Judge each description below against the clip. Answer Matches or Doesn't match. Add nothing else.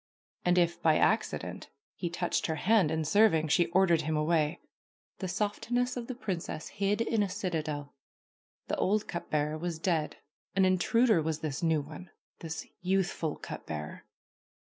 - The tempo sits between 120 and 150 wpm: Doesn't match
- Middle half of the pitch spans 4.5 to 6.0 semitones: Doesn't match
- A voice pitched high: Doesn't match